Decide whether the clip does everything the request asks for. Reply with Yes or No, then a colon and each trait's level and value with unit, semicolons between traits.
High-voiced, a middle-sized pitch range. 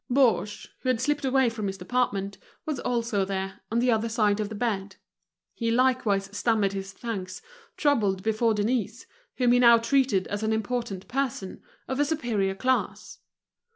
Yes: high, 225 Hz; average, 3.9 semitones